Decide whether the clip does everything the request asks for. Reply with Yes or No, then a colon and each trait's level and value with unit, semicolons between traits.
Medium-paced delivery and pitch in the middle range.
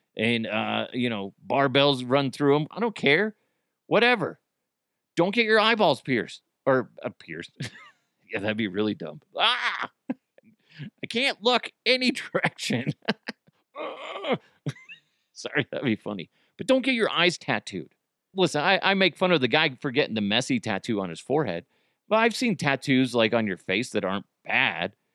Yes: average, 165 wpm; medium, 145 Hz